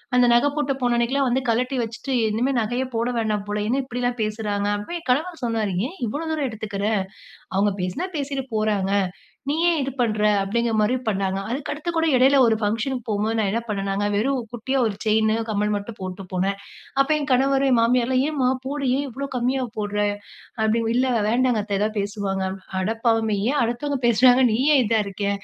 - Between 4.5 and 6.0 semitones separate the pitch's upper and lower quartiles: No, average, 4.0 semitones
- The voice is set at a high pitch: Yes, high, 230 Hz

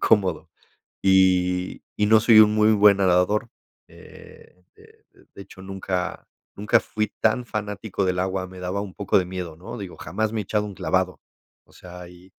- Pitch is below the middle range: Yes, very low, 95 Hz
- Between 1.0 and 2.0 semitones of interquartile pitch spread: No, narrow, 2.6 semitones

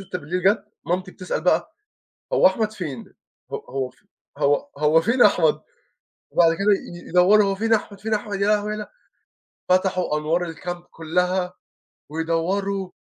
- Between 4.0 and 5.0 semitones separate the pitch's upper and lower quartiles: No, average, 3.6 semitones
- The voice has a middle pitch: Yes, medium, 180 Hz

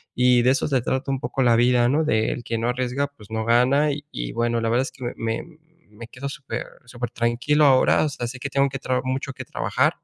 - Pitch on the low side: Yes, low, 125 Hz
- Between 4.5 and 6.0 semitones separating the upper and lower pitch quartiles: No, narrow, 2.5 semitones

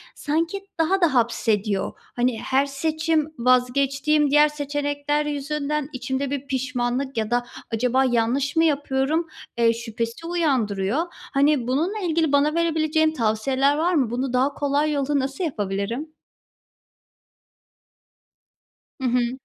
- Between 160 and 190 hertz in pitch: No, very high, 275 Hz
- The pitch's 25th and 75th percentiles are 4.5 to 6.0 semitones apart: No, average, 3.6 semitones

